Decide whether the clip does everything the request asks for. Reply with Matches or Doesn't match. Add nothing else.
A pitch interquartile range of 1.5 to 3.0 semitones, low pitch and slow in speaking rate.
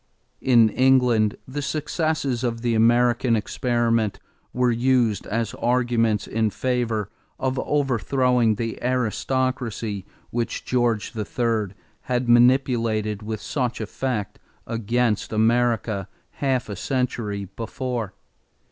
Matches